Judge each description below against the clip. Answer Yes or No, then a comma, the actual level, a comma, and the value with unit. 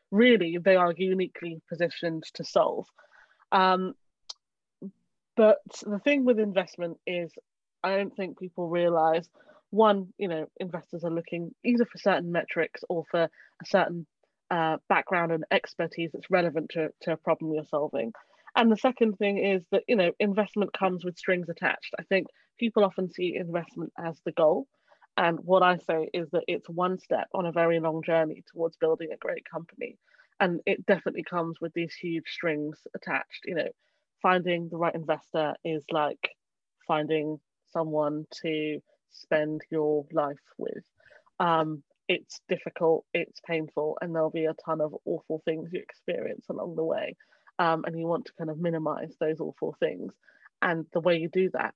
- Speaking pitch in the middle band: Yes, medium, 170 Hz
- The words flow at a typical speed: Yes, average, 170 wpm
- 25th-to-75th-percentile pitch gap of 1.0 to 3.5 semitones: Yes, average, 2.8 semitones